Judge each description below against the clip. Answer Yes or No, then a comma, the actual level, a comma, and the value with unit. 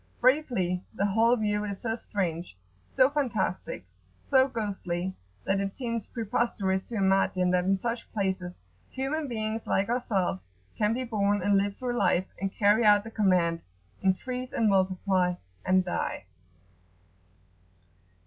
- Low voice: No, high, 205 Hz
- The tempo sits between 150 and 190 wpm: No, average, 140 wpm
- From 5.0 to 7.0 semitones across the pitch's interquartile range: No, average, 3.7 semitones